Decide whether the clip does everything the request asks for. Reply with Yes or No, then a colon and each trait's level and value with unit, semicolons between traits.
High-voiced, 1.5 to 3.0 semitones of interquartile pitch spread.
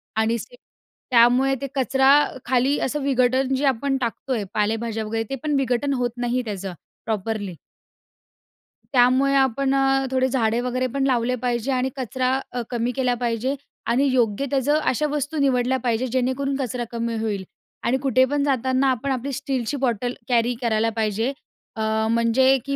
Yes: very high, 255 Hz; narrow, 2.5 semitones